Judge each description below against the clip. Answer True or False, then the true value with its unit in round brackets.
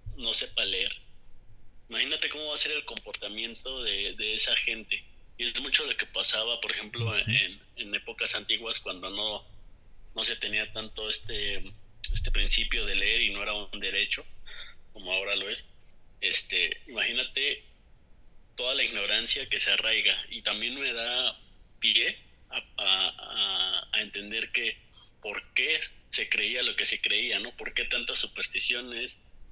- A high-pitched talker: False (110 Hz)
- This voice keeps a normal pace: True (155 wpm)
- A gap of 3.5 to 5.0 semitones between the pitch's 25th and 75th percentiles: False (2.8 semitones)